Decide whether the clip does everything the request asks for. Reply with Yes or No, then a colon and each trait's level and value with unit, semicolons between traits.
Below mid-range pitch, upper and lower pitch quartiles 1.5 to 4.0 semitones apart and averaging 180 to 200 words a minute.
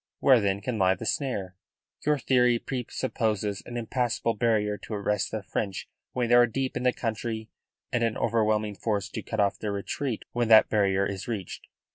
Yes: low, 110 Hz; average, 2.9 semitones; average, 185 wpm